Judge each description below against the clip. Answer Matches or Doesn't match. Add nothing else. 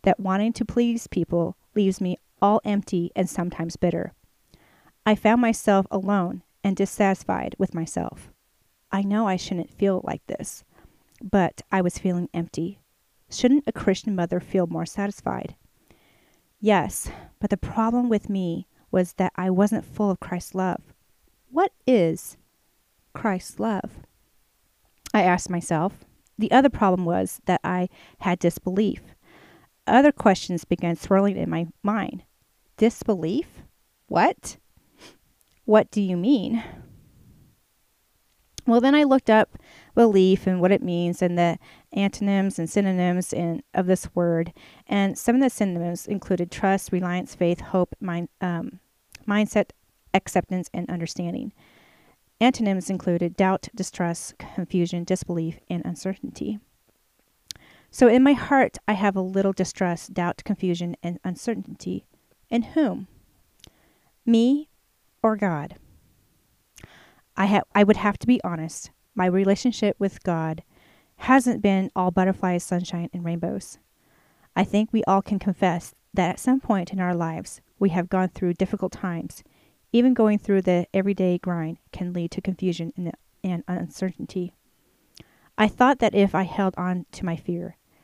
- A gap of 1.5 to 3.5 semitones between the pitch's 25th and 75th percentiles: Matches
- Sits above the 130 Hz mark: Matches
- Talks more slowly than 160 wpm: Matches